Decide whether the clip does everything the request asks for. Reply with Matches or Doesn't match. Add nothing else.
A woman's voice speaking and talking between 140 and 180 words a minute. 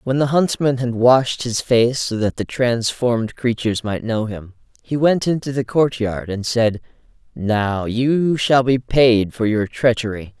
Doesn't match